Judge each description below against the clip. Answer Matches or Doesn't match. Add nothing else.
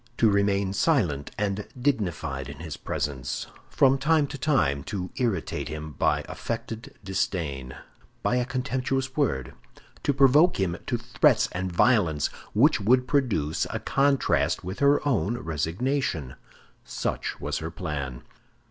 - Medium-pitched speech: Doesn't match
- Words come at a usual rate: Doesn't match